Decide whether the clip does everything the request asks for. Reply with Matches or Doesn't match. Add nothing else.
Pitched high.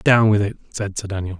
Doesn't match